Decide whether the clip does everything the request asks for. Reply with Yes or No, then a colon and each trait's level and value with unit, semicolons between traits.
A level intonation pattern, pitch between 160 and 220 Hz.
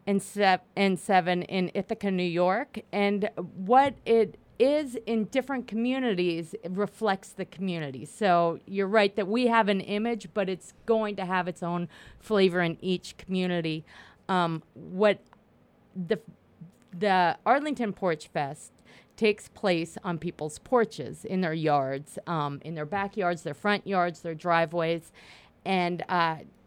No: average, 3.4 semitones; medium, 185 Hz